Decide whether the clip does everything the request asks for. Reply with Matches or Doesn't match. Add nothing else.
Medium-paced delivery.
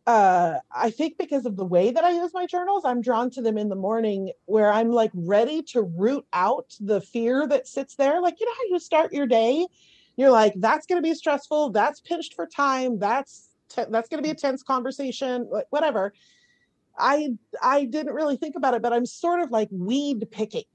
Doesn't match